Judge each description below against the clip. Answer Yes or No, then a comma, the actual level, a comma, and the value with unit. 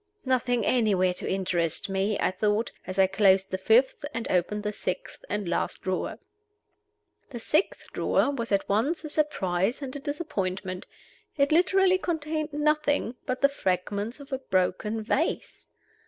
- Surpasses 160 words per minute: No, average, 155 wpm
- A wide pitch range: Yes, wide, 7.1 semitones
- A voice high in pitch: Yes, high, 225 Hz